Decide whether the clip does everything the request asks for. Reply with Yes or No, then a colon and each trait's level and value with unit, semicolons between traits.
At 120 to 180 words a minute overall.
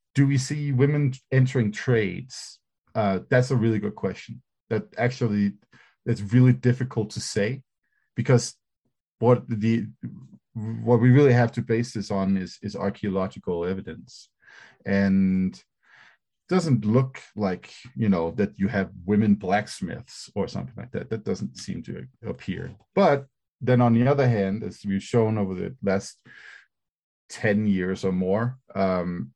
Yes: average, 145 wpm